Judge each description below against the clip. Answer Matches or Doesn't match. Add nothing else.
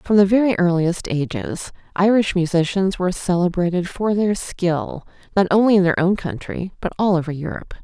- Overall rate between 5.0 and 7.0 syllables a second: Matches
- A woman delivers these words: Matches